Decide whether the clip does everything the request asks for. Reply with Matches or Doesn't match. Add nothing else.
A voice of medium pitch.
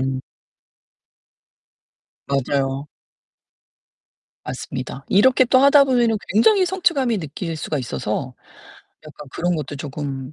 Matches